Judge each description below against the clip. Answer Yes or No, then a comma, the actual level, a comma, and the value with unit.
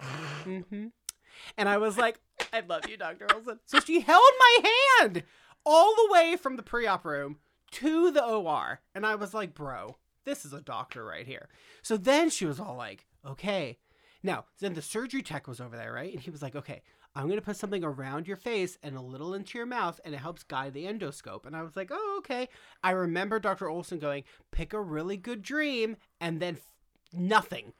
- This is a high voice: Yes, high, 195 Hz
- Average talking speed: No, fast, 210 wpm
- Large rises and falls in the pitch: Yes, wide, 7.6 semitones